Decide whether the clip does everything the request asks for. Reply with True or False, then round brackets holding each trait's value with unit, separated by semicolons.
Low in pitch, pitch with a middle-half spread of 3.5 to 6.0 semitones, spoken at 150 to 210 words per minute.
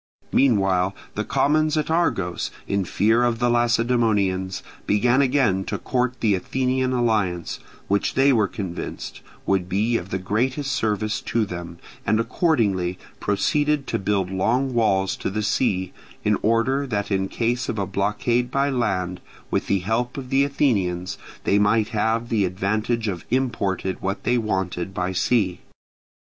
True (110 Hz; 4.4 semitones; 155 wpm)